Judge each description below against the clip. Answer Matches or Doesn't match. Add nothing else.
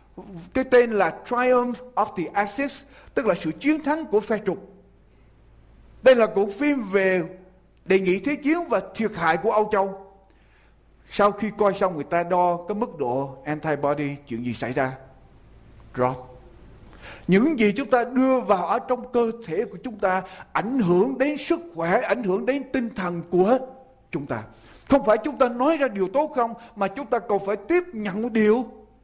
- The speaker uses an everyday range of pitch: Doesn't match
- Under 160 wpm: Doesn't match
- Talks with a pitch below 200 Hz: Doesn't match